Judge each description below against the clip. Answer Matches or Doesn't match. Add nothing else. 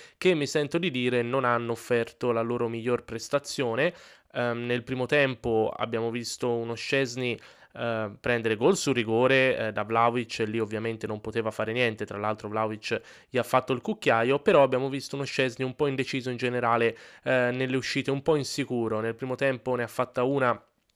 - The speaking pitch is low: Matches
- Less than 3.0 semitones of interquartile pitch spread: Matches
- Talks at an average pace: Doesn't match